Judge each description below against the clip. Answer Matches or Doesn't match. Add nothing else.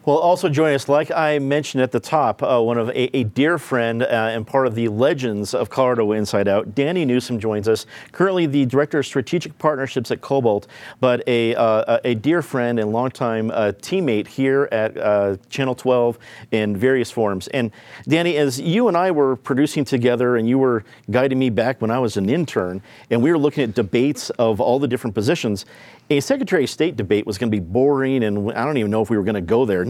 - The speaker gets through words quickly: Matches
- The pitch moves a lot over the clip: Doesn't match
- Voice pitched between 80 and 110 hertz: Doesn't match